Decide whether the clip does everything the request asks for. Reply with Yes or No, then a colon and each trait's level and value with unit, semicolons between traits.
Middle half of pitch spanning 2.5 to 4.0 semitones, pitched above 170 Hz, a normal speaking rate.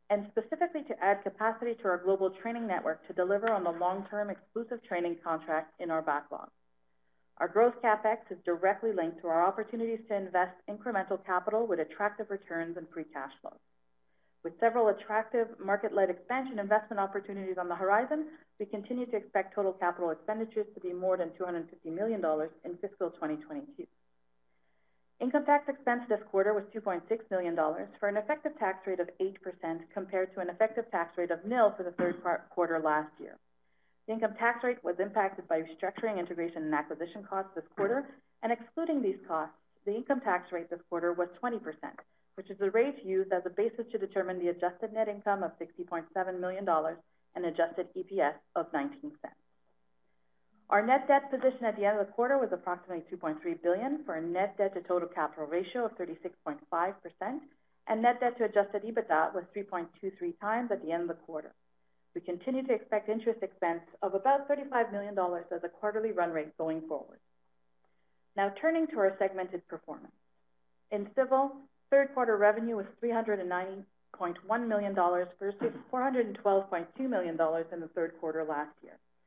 No: average, 4.7 semitones; high, 190 Hz; average, 175 wpm